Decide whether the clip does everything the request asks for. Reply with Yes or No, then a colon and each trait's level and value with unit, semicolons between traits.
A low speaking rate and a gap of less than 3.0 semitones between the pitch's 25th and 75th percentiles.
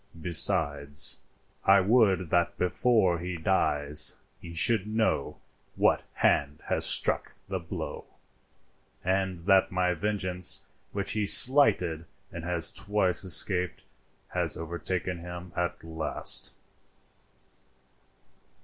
Yes: slow, 105 wpm; narrow, 2.5 semitones